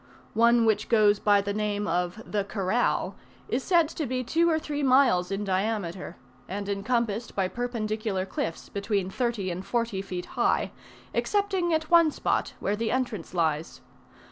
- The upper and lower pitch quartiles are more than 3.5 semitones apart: Yes, average, 4.2 semitones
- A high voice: Yes, high, 215 Hz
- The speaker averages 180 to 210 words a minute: No, average, 160 wpm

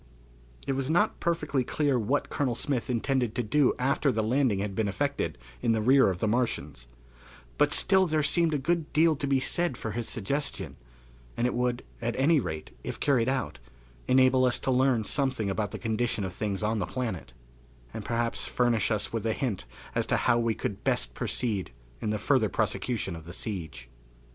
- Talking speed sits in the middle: Yes, average, 195 wpm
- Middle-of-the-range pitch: No, low, 120 Hz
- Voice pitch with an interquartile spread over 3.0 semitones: Yes, average, 4.2 semitones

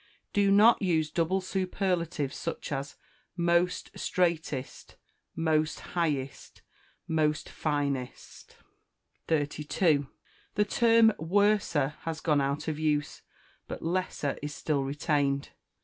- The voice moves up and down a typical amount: Yes, average, 3.7 semitones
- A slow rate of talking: Yes, slow, 100 wpm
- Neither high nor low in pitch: Yes, medium, 160 Hz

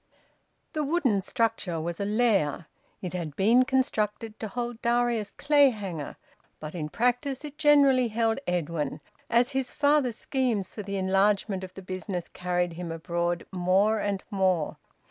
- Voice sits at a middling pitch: No, high, 205 Hz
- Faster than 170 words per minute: No, average, 145 wpm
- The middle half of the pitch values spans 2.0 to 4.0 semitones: No, wide, 5.4 semitones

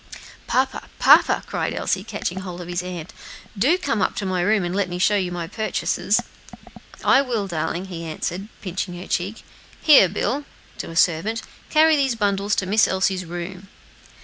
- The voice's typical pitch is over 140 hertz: Yes, high, 190 Hz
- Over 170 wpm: Yes, average, 180 wpm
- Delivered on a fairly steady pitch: No, average, 3.3 semitones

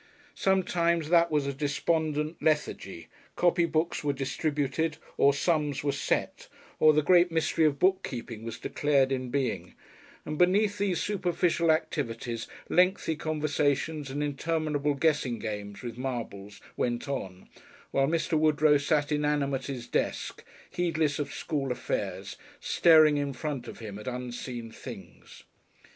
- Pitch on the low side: No, medium, 145 Hz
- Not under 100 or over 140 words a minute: Yes, slow, 135 wpm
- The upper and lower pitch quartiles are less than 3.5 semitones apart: No, average, 3.8 semitones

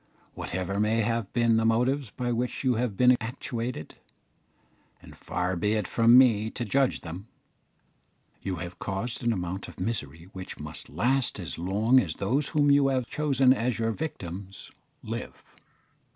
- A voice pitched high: No, low, 115 Hz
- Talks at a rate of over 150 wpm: Yes, average, 160 wpm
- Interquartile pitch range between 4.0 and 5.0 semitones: Yes, average, 4.7 semitones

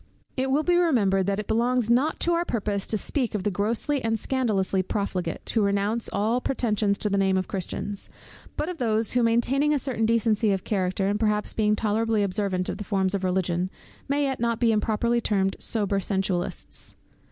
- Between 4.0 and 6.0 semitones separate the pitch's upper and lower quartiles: No, average, 3.2 semitones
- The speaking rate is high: No, average, 195 wpm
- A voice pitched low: No, high, 215 Hz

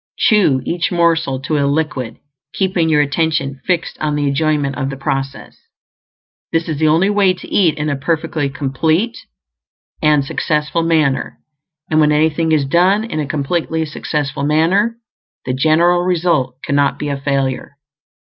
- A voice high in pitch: No, medium, 155 Hz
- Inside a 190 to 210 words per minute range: No, average, 155 wpm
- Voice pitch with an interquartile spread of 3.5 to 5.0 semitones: No, average, 3.1 semitones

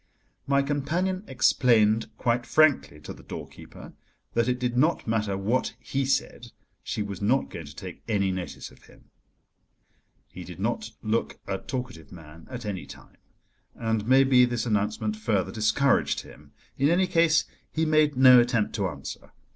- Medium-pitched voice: No, low, 120 Hz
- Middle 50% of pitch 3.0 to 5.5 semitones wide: Yes, average, 4.5 semitones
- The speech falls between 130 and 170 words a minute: Yes, average, 160 wpm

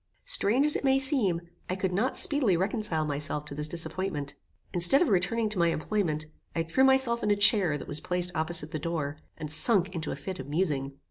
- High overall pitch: No, medium, 180 Hz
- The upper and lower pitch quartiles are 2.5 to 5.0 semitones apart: No, wide, 5.6 semitones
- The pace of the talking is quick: Yes, fast, 210 wpm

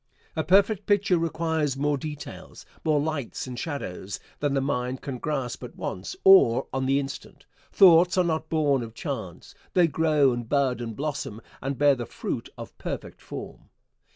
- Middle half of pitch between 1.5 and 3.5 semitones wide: No, average, 3.9 semitones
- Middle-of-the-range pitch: Yes, medium, 145 Hz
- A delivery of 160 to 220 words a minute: Yes, average, 170 wpm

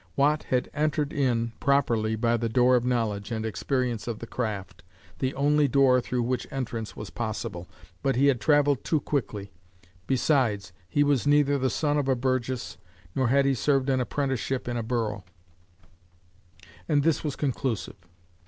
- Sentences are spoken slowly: No, average, 165 wpm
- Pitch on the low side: Yes, low, 130 Hz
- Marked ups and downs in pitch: No, average, 3.5 semitones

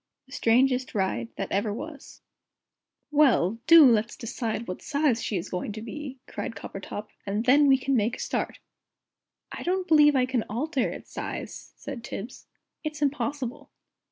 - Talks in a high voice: Yes, very high, 255 Hz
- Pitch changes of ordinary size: Yes, average, 4.7 semitones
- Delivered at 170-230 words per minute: No, average, 160 wpm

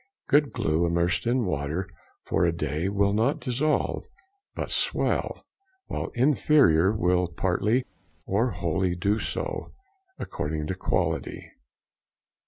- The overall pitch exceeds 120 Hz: No, very low, 95 Hz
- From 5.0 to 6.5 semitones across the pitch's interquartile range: Yes, wide, 5.5 semitones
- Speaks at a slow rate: Yes, slow, 115 wpm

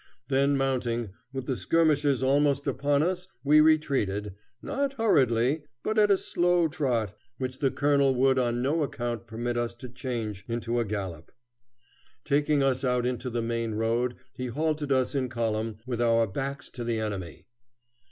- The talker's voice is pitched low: Yes, low, 130 Hz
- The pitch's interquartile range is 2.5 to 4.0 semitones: Yes, average, 3.5 semitones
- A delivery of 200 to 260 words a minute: No, average, 160 wpm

